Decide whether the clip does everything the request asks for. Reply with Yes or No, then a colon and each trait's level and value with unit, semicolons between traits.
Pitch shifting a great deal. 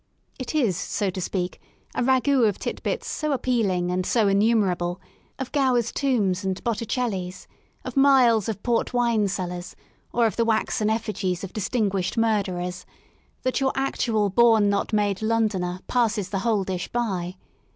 No: average, 4.2 semitones